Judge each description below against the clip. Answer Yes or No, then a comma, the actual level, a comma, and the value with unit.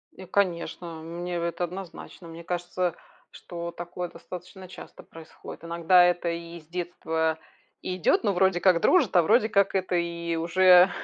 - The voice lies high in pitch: No, medium, 175 Hz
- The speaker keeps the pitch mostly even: Yes, narrow, 1.5 semitones